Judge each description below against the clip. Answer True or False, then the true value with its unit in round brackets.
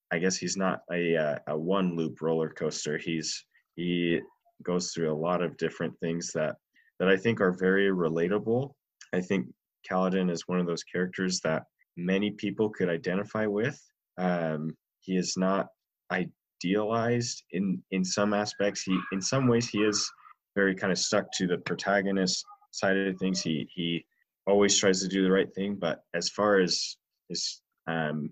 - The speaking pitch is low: True (95 Hz)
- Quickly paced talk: False (170 wpm)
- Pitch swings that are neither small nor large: True (3.0 semitones)